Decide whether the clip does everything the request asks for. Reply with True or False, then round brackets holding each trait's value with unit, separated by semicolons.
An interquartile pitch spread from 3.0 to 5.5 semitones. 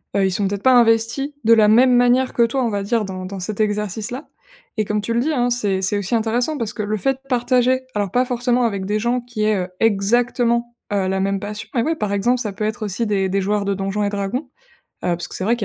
True (3.3 semitones)